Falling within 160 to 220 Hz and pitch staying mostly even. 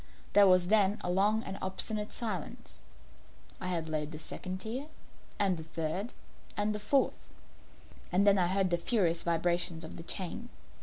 No: high, 190 Hz; average, 3.4 semitones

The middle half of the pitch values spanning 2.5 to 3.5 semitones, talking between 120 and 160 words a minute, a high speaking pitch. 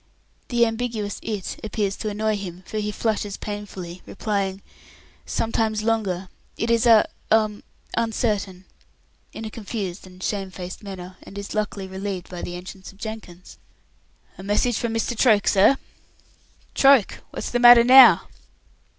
Yes: average, 2.8 semitones; average, 145 wpm; high, 210 Hz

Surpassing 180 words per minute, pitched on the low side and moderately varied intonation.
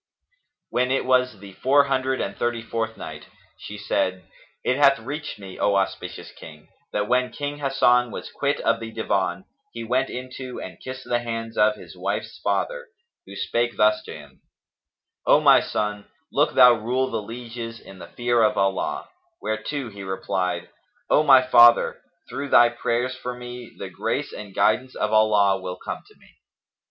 No: average, 175 wpm; low, 115 Hz; average, 3.6 semitones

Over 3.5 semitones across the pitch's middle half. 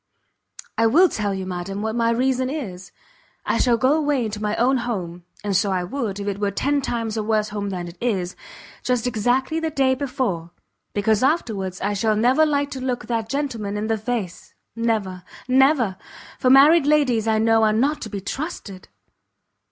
Yes: average, 4.6 semitones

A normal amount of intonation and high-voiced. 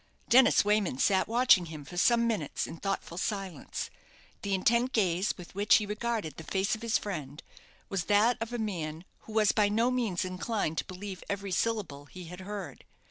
Yes: average, 3.7 semitones; high, 200 Hz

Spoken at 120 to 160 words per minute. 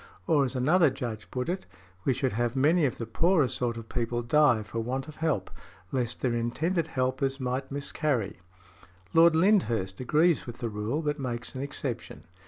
No: average, 180 wpm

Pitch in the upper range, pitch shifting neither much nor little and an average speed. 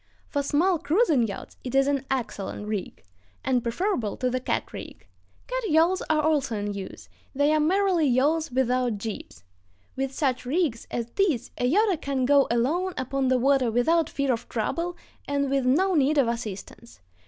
Yes: very high, 270 Hz; average, 4.5 semitones; average, 175 wpm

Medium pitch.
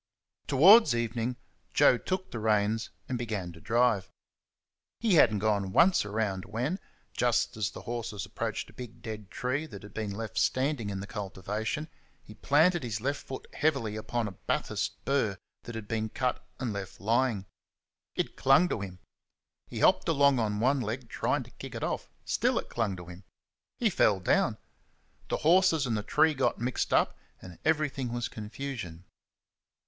No: low, 115 Hz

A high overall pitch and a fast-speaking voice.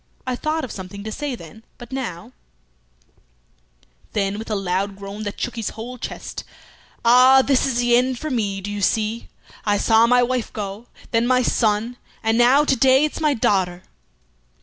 No: high, 225 Hz; average, 185 wpm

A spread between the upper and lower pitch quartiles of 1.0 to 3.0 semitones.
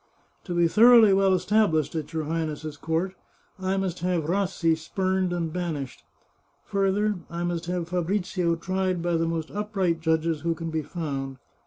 Yes: average, 2.7 semitones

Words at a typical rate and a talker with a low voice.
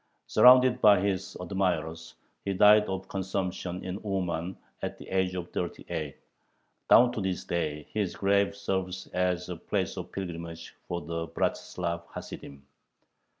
Yes: average, 145 wpm; very low, 90 Hz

